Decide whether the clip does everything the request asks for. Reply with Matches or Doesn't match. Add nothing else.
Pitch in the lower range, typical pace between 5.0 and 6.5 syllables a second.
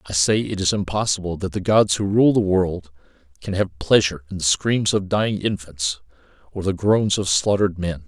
Matches